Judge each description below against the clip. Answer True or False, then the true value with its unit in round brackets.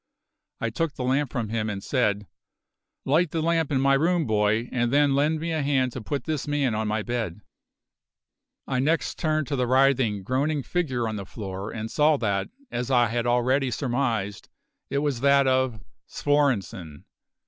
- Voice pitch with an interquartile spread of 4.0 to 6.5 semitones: True (4.5 semitones)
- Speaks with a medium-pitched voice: False (130 Hz)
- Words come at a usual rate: True (180 wpm)